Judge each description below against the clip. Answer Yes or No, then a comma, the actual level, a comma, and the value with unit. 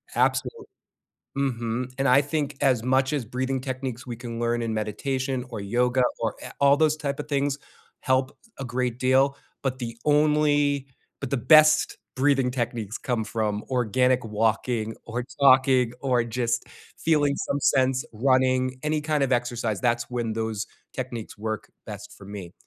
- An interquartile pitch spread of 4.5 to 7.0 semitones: No, average, 2.9 semitones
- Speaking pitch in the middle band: No, low, 130 Hz